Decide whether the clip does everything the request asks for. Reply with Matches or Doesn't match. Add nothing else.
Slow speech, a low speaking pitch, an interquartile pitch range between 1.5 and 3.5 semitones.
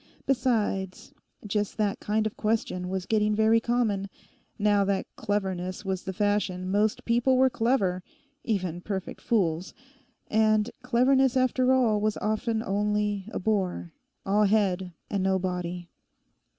Doesn't match